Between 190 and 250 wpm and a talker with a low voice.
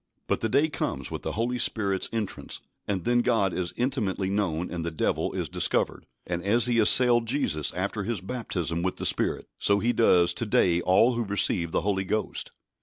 Yes: average, 195 wpm; low, 100 Hz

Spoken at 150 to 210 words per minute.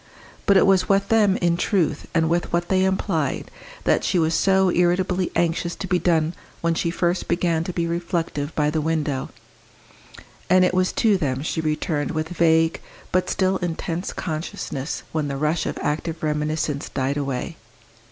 Yes: average, 170 wpm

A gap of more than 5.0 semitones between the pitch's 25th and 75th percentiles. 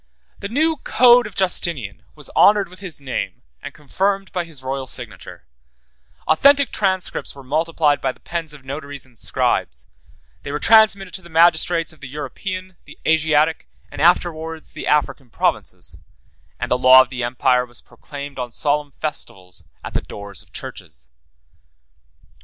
Yes: wide, 5.6 semitones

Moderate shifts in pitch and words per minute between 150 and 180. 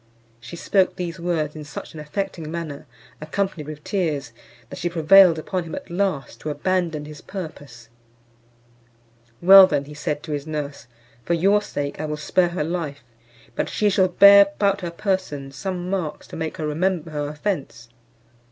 Yes: average, 3.9 semitones; average, 170 wpm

